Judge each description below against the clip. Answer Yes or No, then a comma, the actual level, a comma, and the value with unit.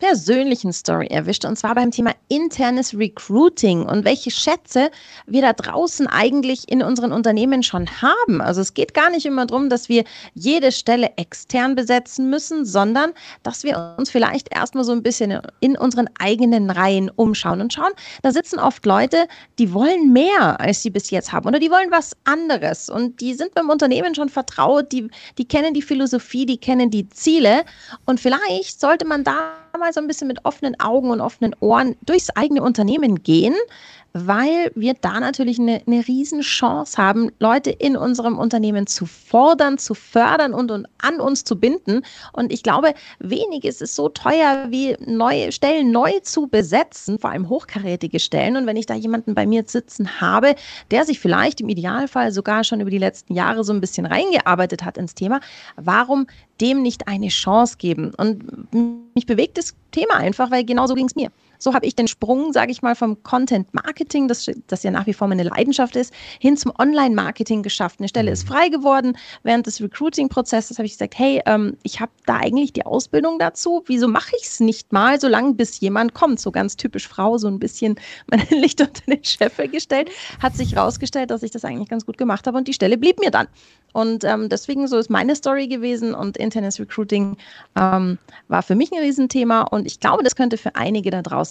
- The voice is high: Yes, high, 245 Hz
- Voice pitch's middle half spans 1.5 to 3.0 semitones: No, average, 4.1 semitones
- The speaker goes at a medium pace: No, fast, 195 wpm